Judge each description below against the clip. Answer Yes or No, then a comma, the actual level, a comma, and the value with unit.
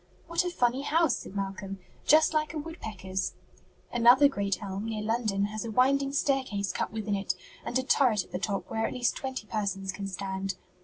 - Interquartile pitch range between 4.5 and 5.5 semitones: Yes, average, 5.2 semitones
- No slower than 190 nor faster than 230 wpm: Yes, average, 195 wpm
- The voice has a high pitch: Yes, high, 220 Hz